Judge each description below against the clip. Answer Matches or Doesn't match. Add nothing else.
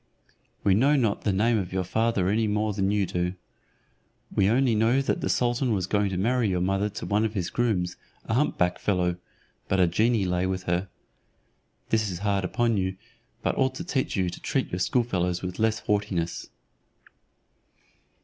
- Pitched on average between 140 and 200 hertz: Doesn't match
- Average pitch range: Matches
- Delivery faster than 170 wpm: Matches